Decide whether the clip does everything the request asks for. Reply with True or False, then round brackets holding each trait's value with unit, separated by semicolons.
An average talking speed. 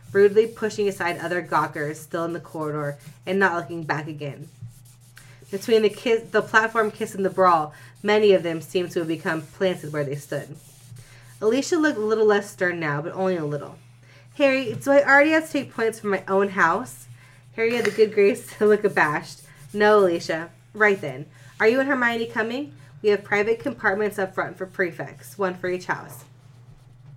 True (190 wpm)